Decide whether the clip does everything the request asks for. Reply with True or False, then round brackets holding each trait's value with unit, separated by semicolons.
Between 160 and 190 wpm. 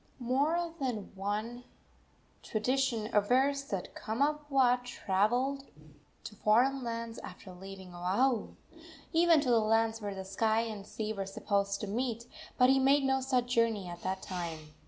False (150 wpm)